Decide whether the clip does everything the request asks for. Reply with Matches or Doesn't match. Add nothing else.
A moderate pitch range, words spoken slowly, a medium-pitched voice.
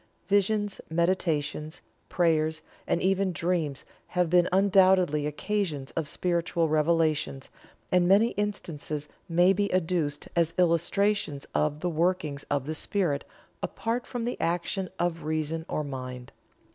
Matches